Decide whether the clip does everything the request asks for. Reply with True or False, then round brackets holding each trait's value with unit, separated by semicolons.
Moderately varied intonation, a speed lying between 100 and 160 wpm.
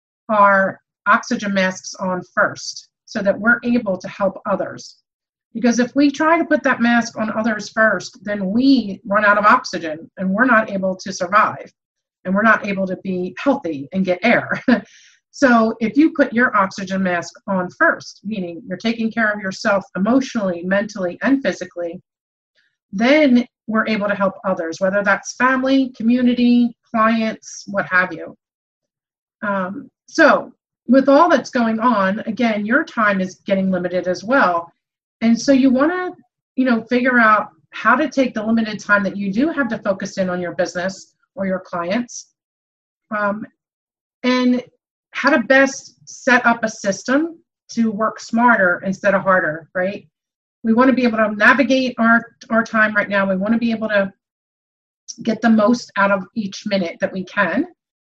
False (4.2 semitones; 170 wpm)